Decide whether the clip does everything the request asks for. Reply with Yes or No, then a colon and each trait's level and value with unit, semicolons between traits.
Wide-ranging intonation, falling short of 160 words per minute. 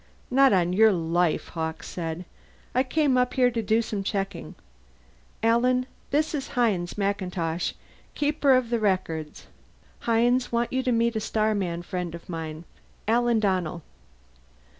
Yes: wide, 5.8 semitones; average, 140 wpm